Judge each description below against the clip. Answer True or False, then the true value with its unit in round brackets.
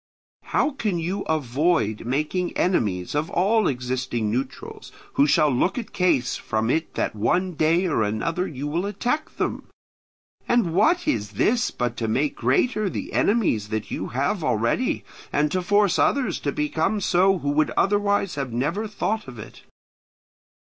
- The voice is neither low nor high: True (160 Hz)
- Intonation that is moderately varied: False (7.8 semitones)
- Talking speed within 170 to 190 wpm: False (160 wpm)